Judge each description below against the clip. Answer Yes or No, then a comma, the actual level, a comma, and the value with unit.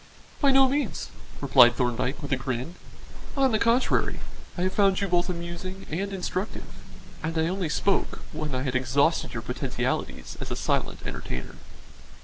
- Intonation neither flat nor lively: No, wide, 6.8 semitones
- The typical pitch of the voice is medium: Yes, medium, 170 Hz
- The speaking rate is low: No, average, 160 wpm